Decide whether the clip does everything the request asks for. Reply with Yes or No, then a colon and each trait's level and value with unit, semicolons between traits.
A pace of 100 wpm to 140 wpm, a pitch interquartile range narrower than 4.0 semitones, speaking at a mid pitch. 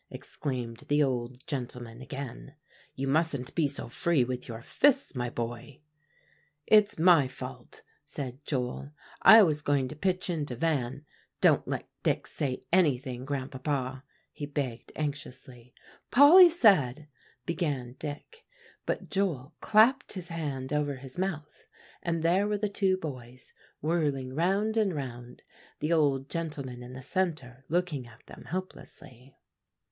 No: slow, 135 wpm; average, 4.9 semitones; medium, 145 Hz